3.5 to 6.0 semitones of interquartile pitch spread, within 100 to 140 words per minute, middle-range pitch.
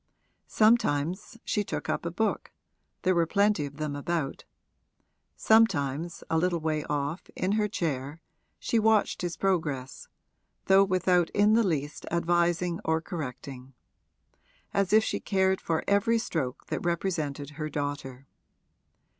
Yes: average, 5.0 semitones; slow, 135 wpm; medium, 170 Hz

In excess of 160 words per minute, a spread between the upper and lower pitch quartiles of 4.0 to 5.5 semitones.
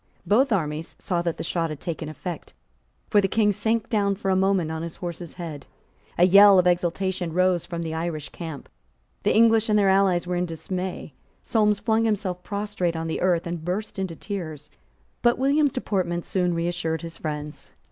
No: average, 190 wpm; average, 3.4 semitones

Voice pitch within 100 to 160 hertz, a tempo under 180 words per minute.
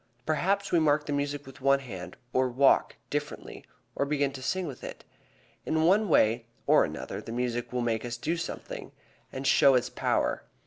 No: medium, 140 Hz; average, 185 wpm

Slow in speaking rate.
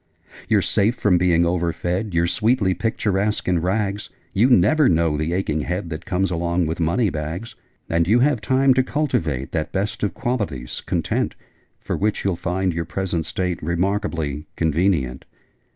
No: average, 160 wpm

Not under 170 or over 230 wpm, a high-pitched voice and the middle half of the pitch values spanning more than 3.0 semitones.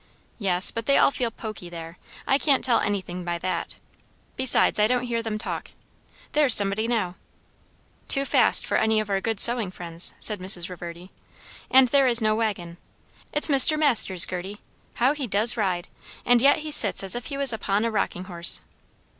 Yes: average, 185 wpm; high, 215 Hz; average, 5.2 semitones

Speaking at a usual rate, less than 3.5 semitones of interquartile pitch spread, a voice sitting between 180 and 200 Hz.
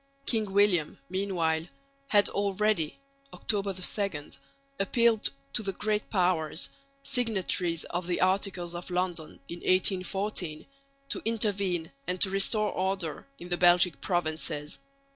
No: slow, 120 wpm; average, 2.7 semitones; medium, 185 Hz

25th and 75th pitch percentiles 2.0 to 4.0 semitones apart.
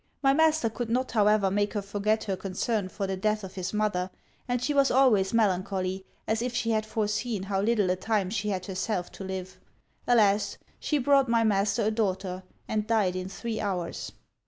Yes: average, 3.1 semitones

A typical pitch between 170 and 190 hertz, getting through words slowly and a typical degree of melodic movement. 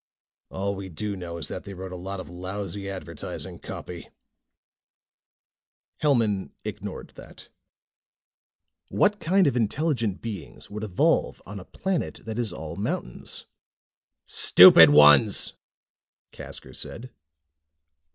No: low, 100 Hz; slow, 115 wpm; average, 4.1 semitones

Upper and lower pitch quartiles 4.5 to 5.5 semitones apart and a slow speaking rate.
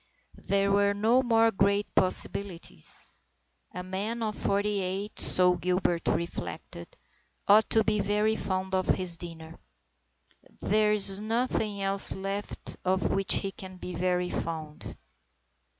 No: narrow, 2.4 semitones; slow, 130 wpm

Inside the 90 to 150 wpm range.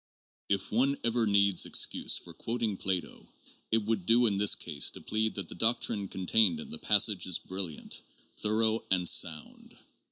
No: average, 165 wpm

